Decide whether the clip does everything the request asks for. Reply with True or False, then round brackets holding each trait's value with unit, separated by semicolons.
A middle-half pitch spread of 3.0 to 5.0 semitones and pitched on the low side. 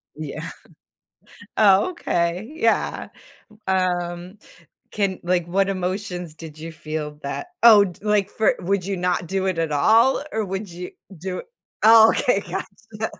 False (3.4 semitones; 185 Hz)